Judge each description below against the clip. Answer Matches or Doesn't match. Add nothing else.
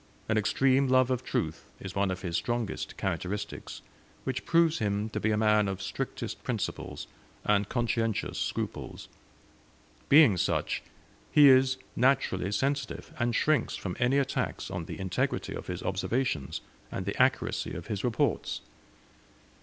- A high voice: Doesn't match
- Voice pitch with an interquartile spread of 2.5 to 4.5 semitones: Doesn't match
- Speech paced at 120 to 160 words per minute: Matches